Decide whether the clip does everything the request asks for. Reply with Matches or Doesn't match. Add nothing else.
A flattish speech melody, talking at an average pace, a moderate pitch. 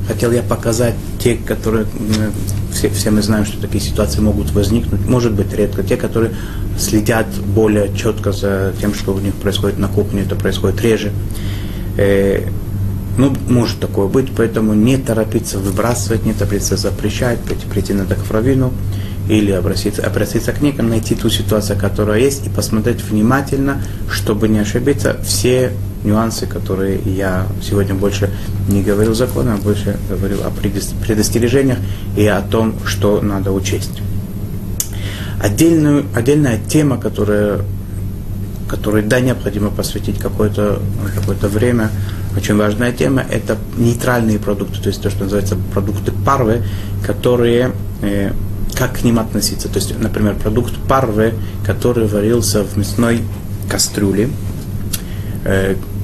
Doesn't match